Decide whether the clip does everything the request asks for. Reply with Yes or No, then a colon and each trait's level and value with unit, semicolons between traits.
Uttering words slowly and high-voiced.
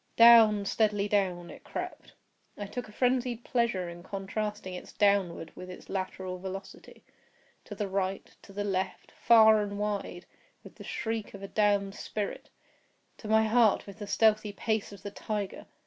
No: average, 150 wpm; high, 205 Hz